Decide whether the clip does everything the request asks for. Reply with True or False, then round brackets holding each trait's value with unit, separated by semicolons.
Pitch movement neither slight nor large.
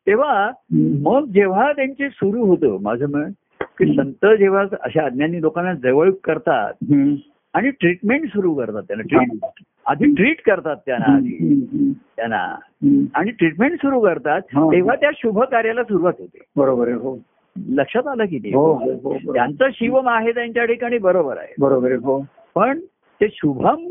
False (8.0 semitones)